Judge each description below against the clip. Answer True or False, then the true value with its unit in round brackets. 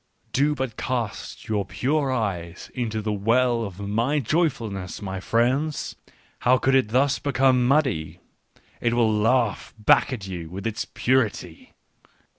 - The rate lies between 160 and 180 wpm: False (145 wpm)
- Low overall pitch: True (115 Hz)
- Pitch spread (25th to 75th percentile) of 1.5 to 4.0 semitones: False (4.4 semitones)